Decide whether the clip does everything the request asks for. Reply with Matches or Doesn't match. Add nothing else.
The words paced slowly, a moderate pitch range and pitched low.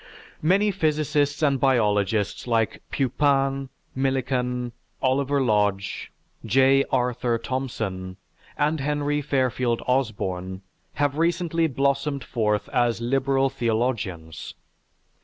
Matches